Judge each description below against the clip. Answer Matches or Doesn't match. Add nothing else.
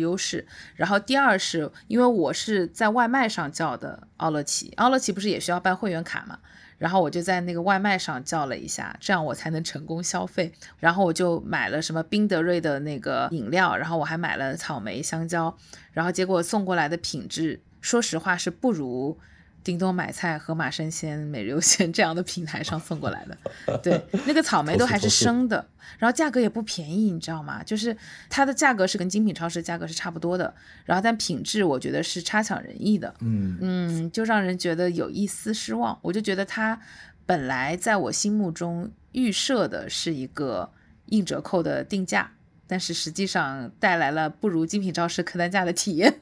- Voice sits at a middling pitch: Matches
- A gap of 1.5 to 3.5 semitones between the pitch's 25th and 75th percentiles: Doesn't match